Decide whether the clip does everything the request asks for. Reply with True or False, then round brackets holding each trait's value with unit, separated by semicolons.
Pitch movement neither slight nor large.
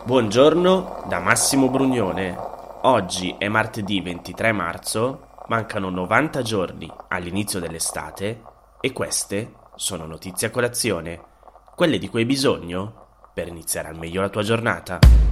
True (4.5 semitones)